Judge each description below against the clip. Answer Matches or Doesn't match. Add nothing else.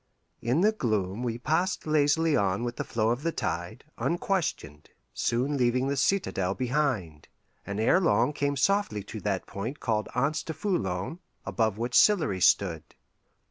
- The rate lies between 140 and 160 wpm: Matches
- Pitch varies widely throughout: Matches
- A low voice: Matches